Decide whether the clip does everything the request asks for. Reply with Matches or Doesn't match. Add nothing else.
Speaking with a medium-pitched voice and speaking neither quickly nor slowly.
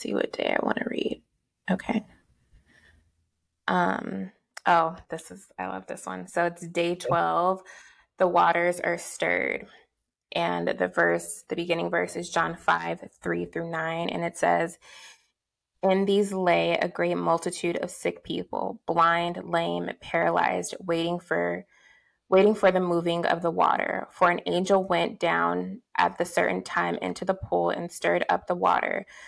Matches